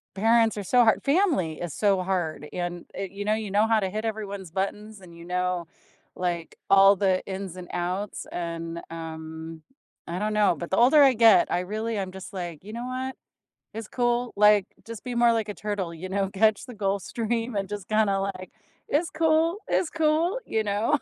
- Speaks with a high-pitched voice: Yes, high, 200 Hz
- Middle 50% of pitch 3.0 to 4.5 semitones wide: Yes, average, 3.8 semitones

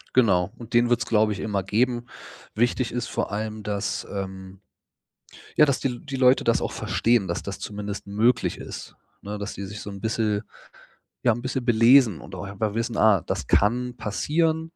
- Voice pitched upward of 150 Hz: No, low, 110 Hz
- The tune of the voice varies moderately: Yes, average, 3.2 semitones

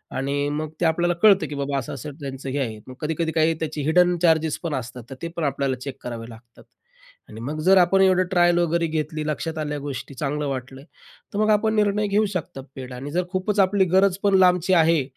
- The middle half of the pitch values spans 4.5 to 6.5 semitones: Yes, average, 4.8 semitones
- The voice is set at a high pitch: No, medium, 155 Hz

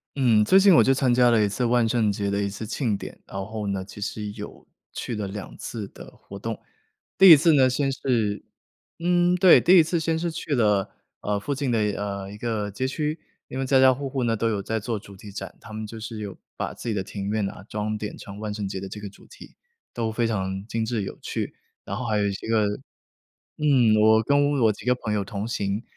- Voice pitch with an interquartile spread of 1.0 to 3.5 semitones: No, average, 4.1 semitones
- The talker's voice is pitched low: Yes, low, 110 Hz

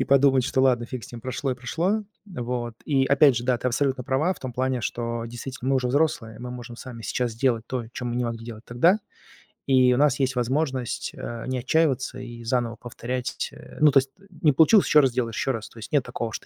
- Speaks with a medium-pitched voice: No, low, 125 Hz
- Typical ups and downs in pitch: No, narrow, 2.3 semitones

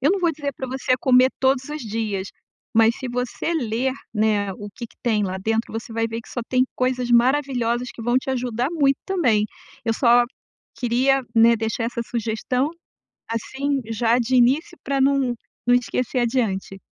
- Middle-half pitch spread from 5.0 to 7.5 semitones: No, average, 2.7 semitones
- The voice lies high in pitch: Yes, high, 245 Hz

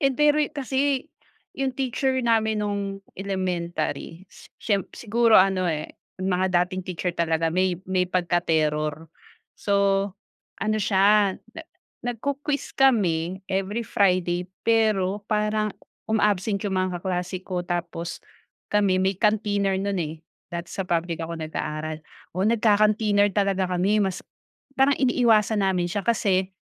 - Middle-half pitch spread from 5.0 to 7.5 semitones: No, average, 3.3 semitones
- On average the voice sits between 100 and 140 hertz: No, high, 195 Hz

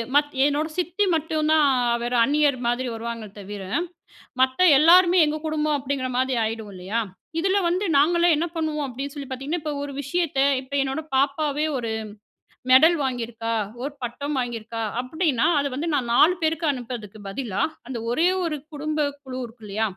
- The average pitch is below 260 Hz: No, very high, 275 Hz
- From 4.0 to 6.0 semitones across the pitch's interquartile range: Yes, average, 4.4 semitones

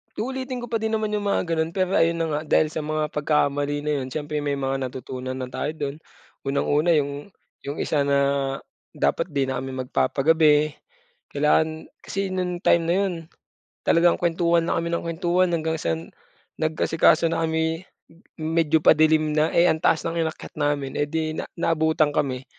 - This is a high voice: No, medium, 155 Hz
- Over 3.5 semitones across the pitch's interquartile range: No, narrow, 2.6 semitones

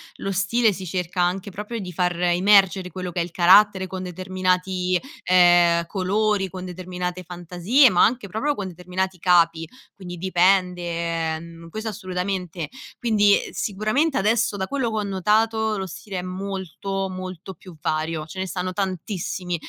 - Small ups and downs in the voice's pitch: Yes, narrow, 2.1 semitones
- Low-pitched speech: No, medium, 185 Hz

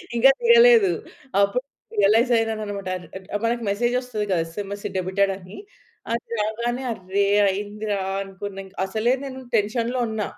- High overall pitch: Yes, high, 210 Hz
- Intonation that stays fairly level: No, average, 3.2 semitones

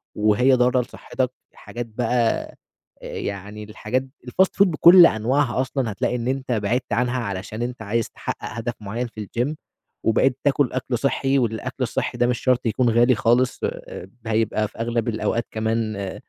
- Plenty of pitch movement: No, average, 2.7 semitones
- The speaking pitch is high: No, low, 120 Hz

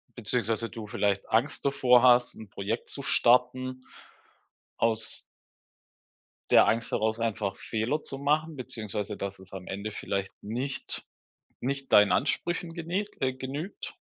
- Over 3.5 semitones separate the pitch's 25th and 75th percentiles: Yes, average, 4.2 semitones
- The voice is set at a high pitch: No, low, 120 Hz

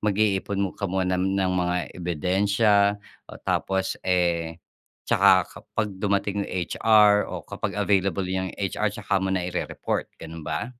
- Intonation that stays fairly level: Yes, narrow, 1.9 semitones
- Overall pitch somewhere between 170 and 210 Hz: No, very low, 95 Hz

